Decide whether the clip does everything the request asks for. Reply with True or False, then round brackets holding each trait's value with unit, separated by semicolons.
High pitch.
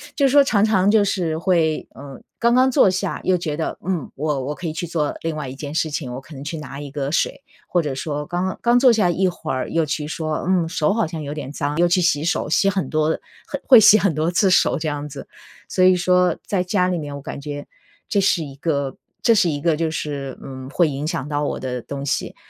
False (160 Hz)